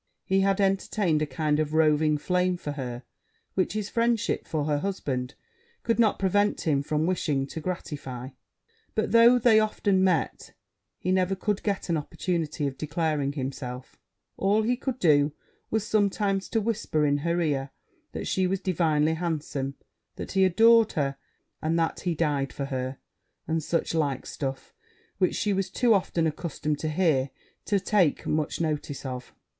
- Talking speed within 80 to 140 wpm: No, average, 165 wpm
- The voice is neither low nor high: Yes, medium, 165 Hz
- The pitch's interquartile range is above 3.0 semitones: Yes, average, 5.0 semitones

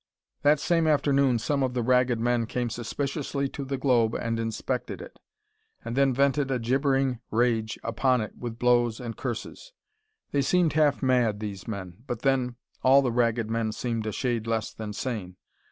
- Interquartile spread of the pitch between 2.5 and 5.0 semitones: Yes, average, 3.1 semitones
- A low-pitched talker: Yes, low, 125 Hz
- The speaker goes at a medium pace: Yes, average, 175 wpm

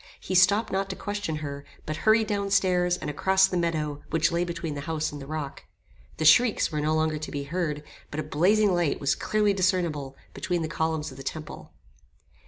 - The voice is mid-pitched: Yes, medium, 165 Hz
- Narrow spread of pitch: No, average, 3.9 semitones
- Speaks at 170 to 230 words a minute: Yes, fast, 205 wpm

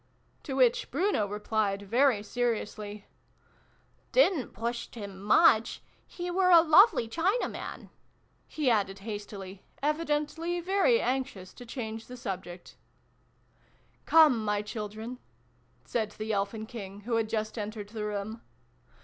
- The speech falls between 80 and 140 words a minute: Yes, slow, 135 wpm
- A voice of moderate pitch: No, high, 225 Hz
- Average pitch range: No, wide, 5.8 semitones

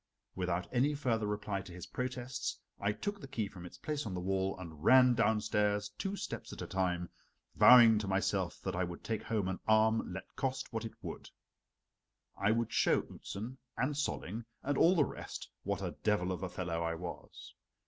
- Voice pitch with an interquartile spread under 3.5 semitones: No, average, 5.0 semitones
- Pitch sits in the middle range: No, low, 105 Hz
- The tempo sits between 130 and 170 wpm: No, average, 195 wpm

